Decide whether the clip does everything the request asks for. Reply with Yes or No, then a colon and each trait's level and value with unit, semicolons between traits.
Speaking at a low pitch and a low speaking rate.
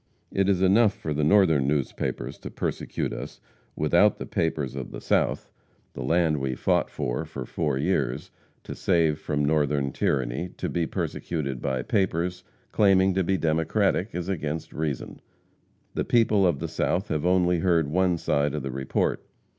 No: very low, 80 Hz; average, 165 wpm